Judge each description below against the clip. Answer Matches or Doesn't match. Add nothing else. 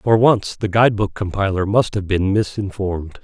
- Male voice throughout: Matches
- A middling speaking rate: Matches